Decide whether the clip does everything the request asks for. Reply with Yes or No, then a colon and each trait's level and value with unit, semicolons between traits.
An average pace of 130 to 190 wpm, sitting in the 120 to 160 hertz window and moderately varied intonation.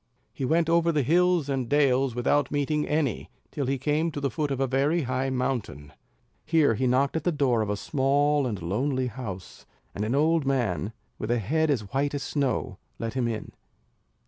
No: average, 200 wpm; low, 135 Hz; average, 3.4 semitones